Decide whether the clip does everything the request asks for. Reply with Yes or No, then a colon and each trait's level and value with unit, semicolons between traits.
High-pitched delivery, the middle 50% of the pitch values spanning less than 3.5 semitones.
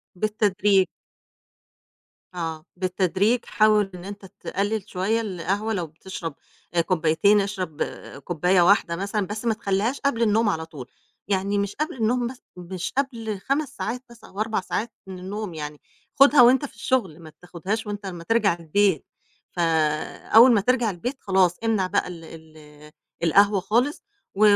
No: high, 200 Hz; average, 4.1 semitones